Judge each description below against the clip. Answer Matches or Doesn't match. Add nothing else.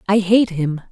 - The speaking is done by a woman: Matches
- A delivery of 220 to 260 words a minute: Doesn't match